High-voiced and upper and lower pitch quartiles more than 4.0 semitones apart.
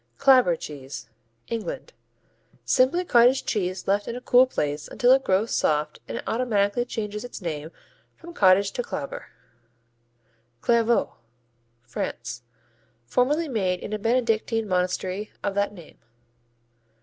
Yes: high, 210 Hz; average, 5.3 semitones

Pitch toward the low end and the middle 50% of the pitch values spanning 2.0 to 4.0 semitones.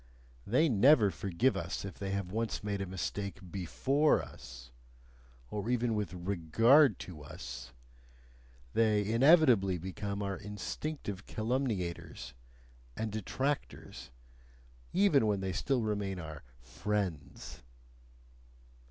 No: low, 100 Hz; average, 4.4 semitones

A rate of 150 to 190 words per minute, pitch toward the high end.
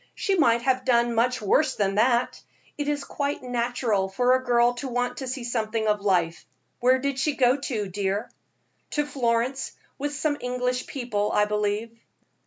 Yes: average, 175 wpm; high, 245 Hz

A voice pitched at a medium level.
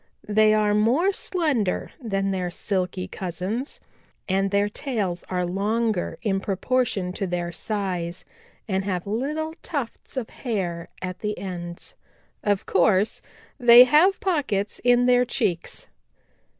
No: high, 205 Hz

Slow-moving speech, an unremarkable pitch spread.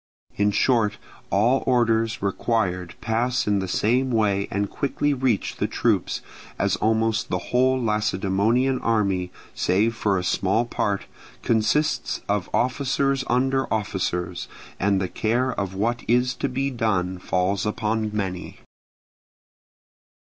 Yes: slow, 130 wpm; average, 4.0 semitones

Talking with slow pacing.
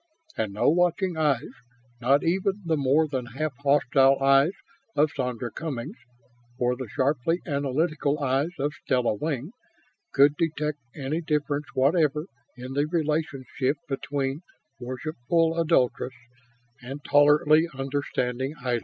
Yes: slow, 120 wpm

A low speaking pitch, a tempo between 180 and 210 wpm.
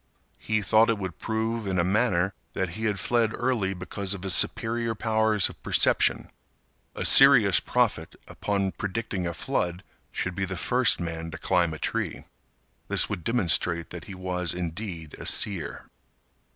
No: very low, 95 Hz; average, 165 wpm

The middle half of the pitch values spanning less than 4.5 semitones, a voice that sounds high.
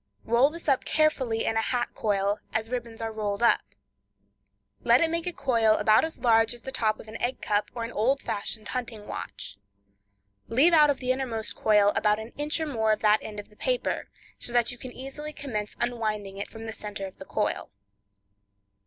Yes: average, 3.5 semitones; high, 230 Hz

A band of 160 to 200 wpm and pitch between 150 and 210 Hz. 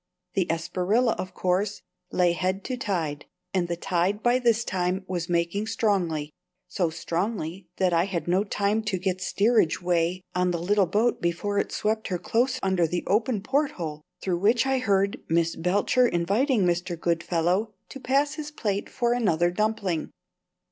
Yes: average, 165 wpm; high, 190 Hz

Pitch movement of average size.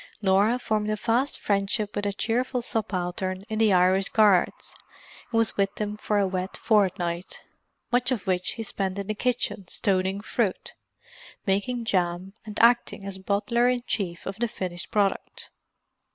Yes: average, 3.0 semitones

